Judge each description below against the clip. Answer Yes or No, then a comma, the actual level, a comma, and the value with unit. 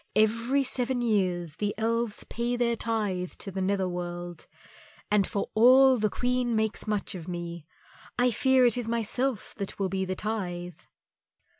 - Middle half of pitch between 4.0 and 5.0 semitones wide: Yes, average, 4.4 semitones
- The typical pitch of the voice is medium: No, high, 215 Hz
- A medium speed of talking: Yes, average, 160 wpm